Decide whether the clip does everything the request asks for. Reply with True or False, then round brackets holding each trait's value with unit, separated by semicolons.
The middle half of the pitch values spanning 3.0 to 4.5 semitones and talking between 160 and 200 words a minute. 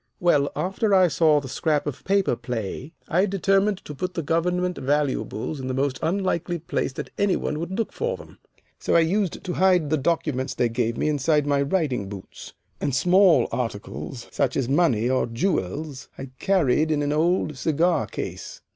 False (5.2 semitones; 180 wpm)